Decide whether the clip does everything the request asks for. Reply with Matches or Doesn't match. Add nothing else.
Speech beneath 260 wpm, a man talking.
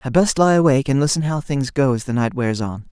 Doesn't match